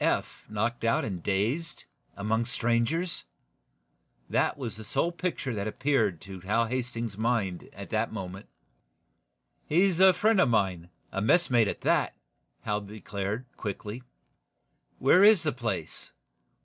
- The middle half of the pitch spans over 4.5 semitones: Yes, average, 5.2 semitones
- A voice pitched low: Yes, low, 115 Hz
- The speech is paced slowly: Yes, slow, 130 wpm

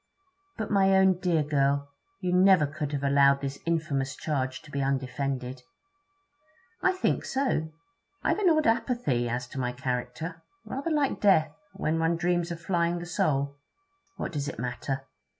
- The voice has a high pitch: No, medium, 155 Hz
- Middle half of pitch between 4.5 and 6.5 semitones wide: Yes, average, 4.9 semitones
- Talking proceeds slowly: No, average, 160 wpm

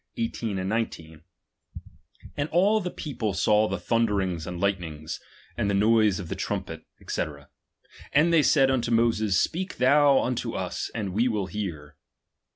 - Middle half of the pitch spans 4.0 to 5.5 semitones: Yes, average, 5.2 semitones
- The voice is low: Yes, low, 110 Hz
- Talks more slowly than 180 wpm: Yes, average, 140 wpm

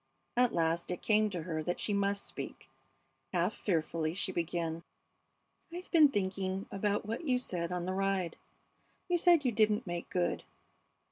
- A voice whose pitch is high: Yes, high, 195 Hz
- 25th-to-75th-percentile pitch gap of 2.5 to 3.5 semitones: No, average, 3.9 semitones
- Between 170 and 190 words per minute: No, average, 160 wpm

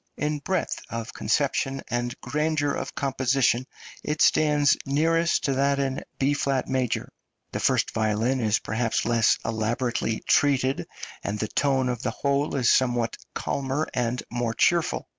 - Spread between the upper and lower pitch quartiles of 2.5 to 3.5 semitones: Yes, average, 3.2 semitones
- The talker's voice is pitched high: No, low, 135 Hz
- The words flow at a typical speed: Yes, average, 145 wpm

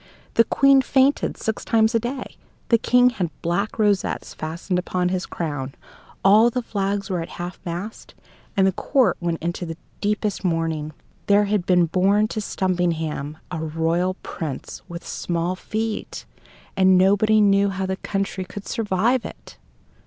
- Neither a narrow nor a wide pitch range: Yes, average, 3.7 semitones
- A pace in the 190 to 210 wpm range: No, average, 155 wpm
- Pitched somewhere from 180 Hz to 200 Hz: Yes, high, 190 Hz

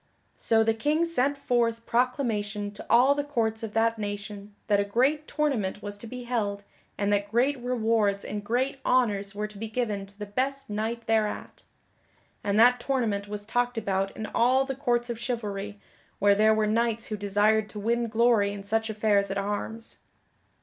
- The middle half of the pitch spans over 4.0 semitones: No, average, 2.9 semitones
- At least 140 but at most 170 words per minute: No, average, 185 wpm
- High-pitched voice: Yes, high, 220 Hz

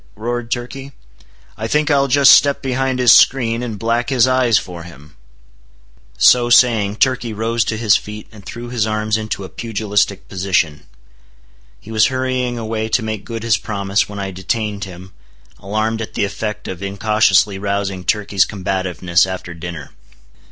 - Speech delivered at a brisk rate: No, average, 160 wpm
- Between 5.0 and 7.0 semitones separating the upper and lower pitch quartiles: No, average, 3.5 semitones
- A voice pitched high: No, low, 110 Hz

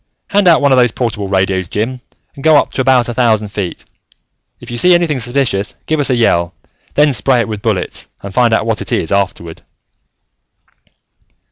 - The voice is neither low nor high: No, low, 120 Hz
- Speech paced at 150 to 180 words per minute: No, average, 195 wpm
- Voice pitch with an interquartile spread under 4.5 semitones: No, average, 5.1 semitones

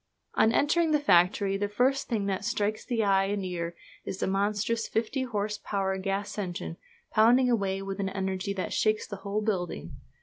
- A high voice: Yes, high, 200 Hz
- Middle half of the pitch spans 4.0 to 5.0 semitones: No, narrow, 2.4 semitones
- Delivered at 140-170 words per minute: No, average, 180 wpm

